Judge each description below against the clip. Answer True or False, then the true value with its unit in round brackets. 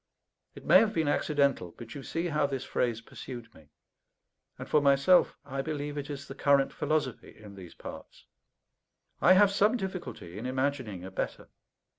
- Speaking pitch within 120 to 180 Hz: True (140 Hz)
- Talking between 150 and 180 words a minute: True (170 wpm)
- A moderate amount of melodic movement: True (4.5 semitones)